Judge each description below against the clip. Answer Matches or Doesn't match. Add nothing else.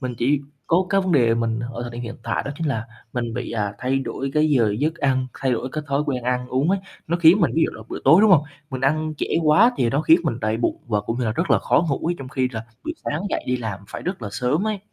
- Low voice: Matches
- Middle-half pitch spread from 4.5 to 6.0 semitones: Matches